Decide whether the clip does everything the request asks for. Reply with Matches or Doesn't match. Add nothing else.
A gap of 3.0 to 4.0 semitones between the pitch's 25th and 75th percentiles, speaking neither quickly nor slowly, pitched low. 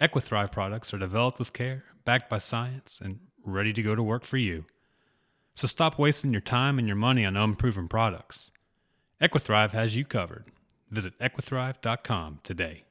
Matches